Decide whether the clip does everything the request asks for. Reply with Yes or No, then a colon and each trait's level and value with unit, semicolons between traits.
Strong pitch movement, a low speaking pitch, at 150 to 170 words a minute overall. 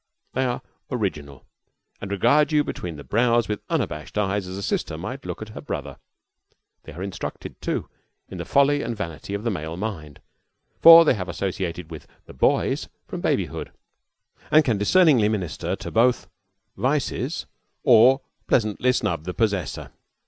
Yes: wide, 5.9 semitones; low, 105 Hz; average, 160 wpm